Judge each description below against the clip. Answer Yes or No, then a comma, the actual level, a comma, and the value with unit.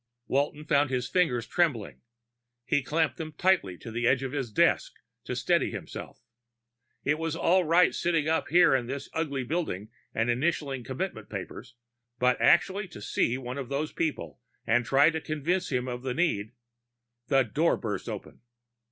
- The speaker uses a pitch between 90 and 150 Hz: Yes, medium, 140 Hz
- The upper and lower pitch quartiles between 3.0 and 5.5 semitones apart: Yes, average, 4.9 semitones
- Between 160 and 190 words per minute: Yes, average, 170 wpm